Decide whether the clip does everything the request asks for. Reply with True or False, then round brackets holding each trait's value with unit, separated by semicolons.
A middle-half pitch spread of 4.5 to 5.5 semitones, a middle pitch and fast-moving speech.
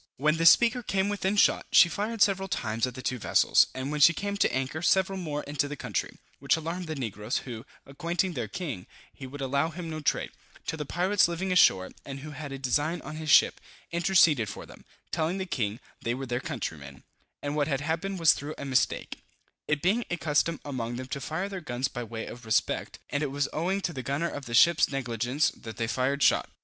True (5.0 semitones; 150 Hz; 225 wpm)